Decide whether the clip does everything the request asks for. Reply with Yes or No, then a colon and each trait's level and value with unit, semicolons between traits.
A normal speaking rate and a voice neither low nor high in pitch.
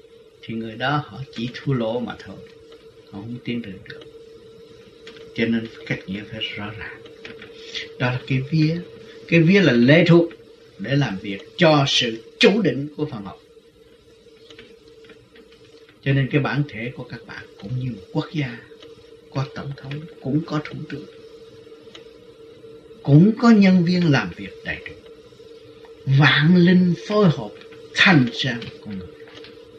No: slow, 155 wpm; medium, 170 Hz